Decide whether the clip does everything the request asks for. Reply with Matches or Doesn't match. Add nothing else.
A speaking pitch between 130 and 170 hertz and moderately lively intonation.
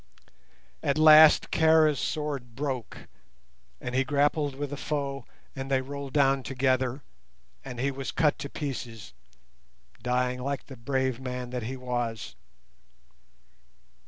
Doesn't match